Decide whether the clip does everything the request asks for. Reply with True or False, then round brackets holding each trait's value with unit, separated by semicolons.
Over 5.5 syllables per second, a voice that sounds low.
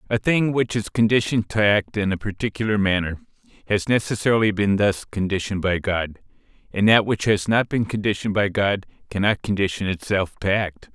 True (5.7 syllables/s; 105 Hz)